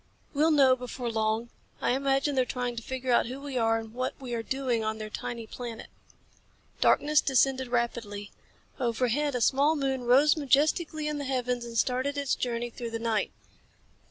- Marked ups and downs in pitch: No, average, 2.8 semitones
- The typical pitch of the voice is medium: No, very high, 250 Hz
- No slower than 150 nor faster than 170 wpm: No, average, 180 wpm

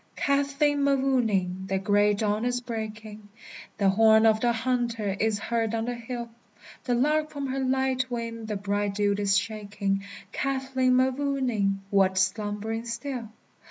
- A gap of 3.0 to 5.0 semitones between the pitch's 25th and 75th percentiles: Yes, average, 3.9 semitones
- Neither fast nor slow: Yes, average, 145 wpm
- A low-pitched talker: No, high, 225 Hz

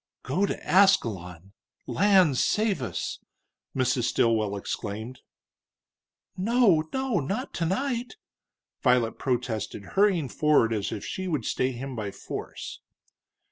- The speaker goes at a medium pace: No, slow, 110 wpm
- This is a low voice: Yes, low, 130 Hz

